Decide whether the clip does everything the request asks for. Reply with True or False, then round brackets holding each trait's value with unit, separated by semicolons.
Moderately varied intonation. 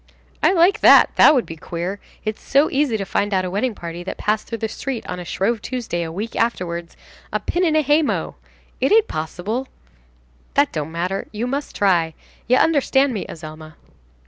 False (7.5 semitones)